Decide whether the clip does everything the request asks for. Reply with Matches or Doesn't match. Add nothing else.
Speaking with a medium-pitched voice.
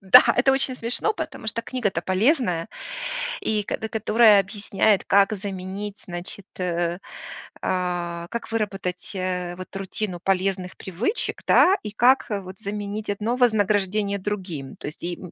Doesn't match